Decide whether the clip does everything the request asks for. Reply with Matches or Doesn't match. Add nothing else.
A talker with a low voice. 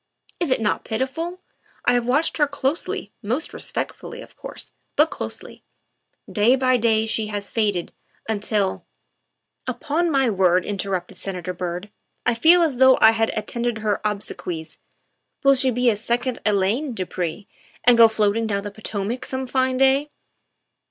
Doesn't match